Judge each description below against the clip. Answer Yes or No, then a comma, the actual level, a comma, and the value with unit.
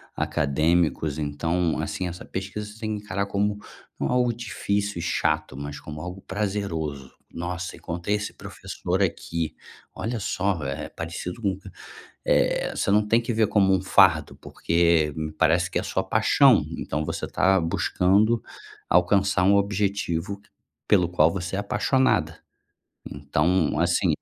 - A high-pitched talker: No, very low, 90 Hz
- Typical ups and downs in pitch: Yes, average, 3.9 semitones